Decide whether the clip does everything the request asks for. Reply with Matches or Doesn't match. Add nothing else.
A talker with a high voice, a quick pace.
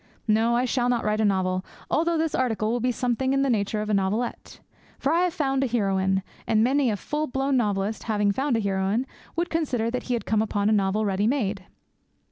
Matches